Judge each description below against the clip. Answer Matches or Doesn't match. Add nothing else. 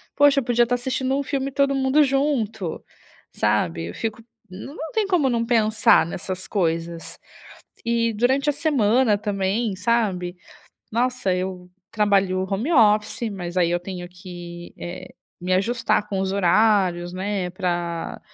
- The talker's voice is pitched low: Doesn't match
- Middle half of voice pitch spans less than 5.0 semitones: Doesn't match